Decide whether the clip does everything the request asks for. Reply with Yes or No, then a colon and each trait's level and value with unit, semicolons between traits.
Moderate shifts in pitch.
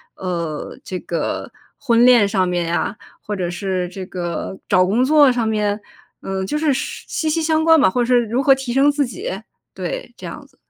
No: wide, 6.9 semitones